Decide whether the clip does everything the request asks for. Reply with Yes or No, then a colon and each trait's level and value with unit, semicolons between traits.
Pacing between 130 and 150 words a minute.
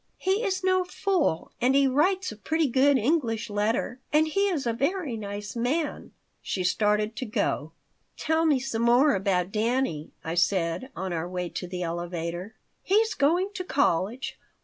No: average, 170 wpm